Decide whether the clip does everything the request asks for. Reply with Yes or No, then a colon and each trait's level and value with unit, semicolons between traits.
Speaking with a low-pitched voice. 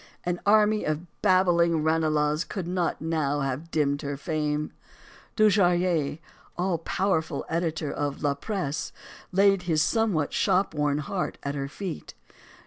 No: medium, 165 Hz